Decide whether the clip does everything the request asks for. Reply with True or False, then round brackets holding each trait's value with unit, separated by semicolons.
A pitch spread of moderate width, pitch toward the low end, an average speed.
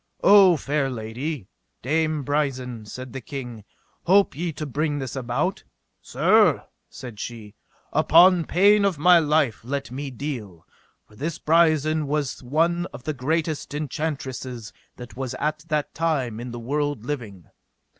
False (4.2 semitones; 145 Hz; 145 wpm)